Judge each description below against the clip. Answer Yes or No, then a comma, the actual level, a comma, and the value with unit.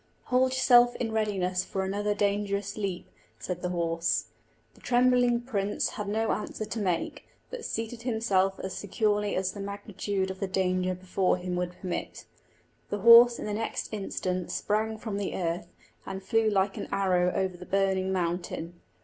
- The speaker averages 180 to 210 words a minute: No, average, 165 wpm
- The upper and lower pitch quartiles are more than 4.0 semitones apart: No, average, 2.9 semitones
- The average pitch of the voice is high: Yes, high, 200 Hz